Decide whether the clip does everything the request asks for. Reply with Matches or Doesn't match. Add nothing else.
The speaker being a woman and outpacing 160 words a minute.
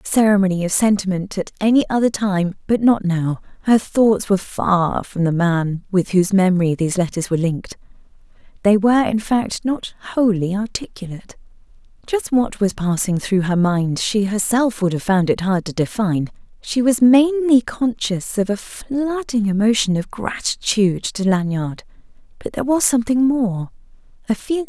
Matches